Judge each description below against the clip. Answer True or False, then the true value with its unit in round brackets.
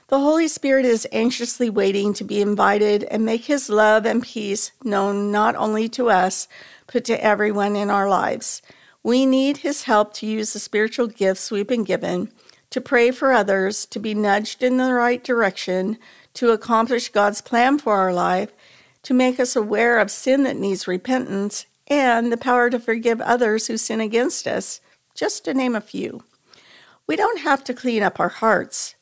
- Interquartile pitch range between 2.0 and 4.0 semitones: True (3.3 semitones)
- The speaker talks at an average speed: True (180 wpm)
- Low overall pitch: False (225 Hz)